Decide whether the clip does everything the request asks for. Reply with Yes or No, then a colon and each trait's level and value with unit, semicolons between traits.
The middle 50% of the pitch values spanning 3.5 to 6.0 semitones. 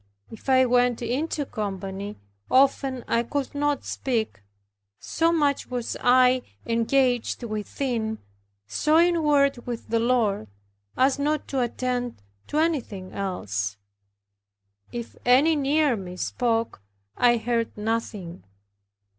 Yes: average, 4.0 semitones